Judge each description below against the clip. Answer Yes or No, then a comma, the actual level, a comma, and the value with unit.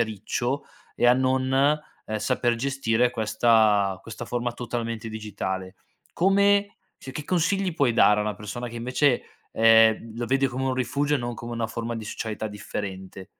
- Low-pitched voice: Yes, low, 120 Hz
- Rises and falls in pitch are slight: No, average, 3.3 semitones